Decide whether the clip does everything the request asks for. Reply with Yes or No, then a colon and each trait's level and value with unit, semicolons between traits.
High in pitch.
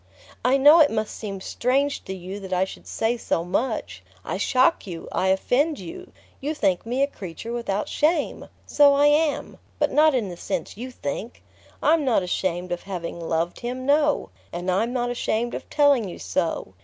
Yes: high, 235 Hz